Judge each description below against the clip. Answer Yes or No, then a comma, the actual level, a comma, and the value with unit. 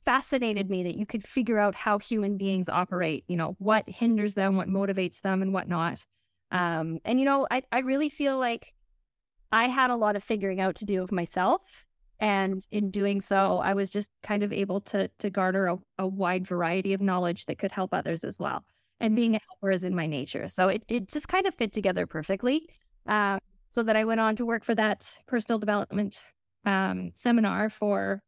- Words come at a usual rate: No, fast, 210 wpm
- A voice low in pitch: No, high, 200 Hz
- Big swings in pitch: No, average, 3.1 semitones